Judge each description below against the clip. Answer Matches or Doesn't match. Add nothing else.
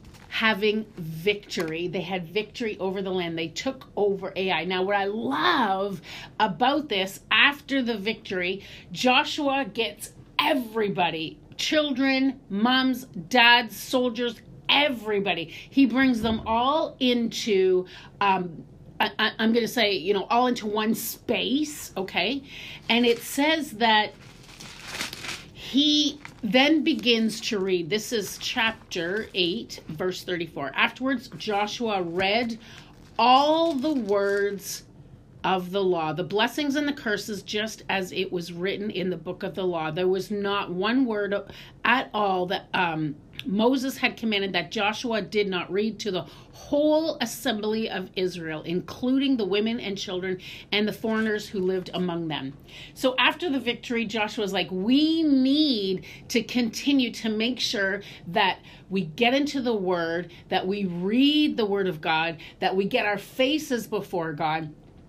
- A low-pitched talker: Doesn't match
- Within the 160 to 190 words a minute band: Doesn't match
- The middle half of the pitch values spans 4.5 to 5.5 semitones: Matches